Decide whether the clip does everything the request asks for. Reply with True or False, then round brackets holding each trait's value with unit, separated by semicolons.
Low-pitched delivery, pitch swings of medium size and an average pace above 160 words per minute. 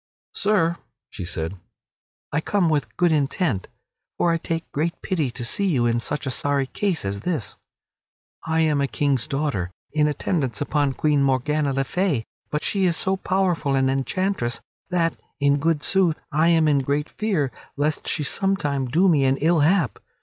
False (150 Hz; 3.9 semitones; 180 wpm)